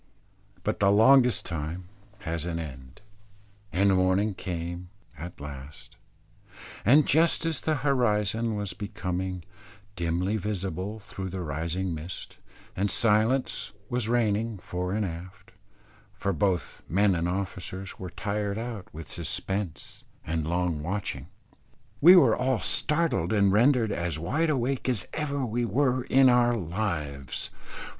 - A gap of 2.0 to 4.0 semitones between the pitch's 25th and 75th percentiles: No, average, 5.1 semitones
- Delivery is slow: Yes, slow, 130 wpm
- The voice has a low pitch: Yes, low, 100 Hz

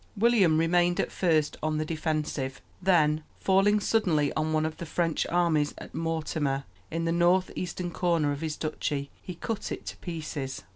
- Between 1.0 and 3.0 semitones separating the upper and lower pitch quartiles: Yes, narrow, 2.4 semitones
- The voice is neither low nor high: Yes, medium, 165 Hz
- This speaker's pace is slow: No, average, 175 wpm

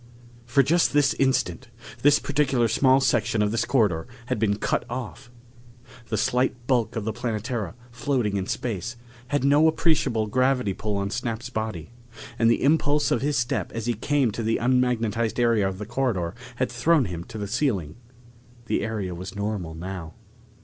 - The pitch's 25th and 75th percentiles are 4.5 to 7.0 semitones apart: No, average, 3.8 semitones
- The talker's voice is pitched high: No, low, 115 Hz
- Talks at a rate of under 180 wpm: Yes, average, 170 wpm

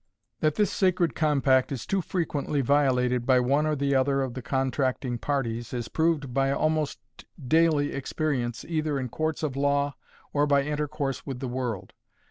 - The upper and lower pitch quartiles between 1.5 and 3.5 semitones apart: Yes, average, 2.8 semitones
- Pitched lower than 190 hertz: Yes, medium, 140 Hz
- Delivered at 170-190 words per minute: No, average, 160 wpm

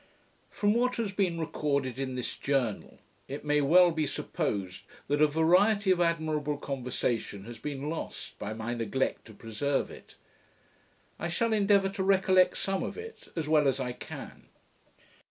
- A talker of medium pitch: Yes, medium, 150 Hz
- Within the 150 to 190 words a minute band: Yes, average, 160 wpm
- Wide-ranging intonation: Yes, wide, 6.0 semitones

